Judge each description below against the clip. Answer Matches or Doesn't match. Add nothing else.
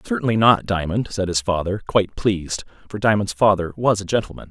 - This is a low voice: Matches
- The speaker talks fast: Doesn't match